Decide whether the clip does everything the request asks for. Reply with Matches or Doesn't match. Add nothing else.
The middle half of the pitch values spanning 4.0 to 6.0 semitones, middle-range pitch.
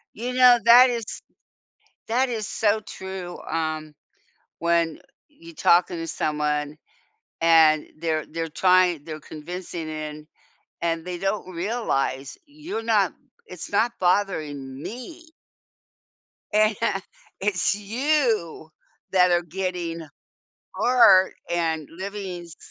Matches